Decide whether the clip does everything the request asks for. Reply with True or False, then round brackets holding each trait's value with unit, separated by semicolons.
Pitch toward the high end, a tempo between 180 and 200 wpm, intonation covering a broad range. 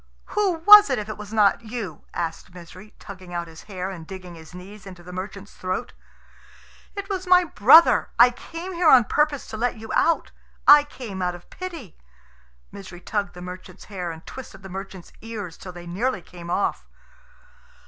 True (200 Hz; 185 wpm; 5.7 semitones)